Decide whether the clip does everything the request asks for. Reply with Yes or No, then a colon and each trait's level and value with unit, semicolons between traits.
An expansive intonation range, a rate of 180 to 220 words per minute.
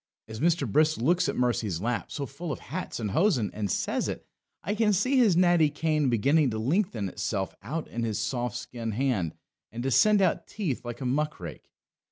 Yes: wide, 6.8 semitones; fast, 205 wpm